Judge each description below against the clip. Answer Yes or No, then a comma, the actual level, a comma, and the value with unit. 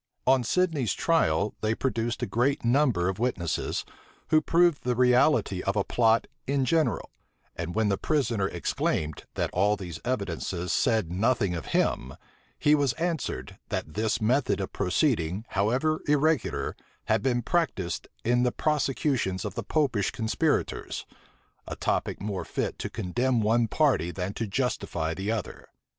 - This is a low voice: Yes, low, 115 Hz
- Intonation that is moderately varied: No, wide, 5.8 semitones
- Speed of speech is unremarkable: Yes, average, 150 wpm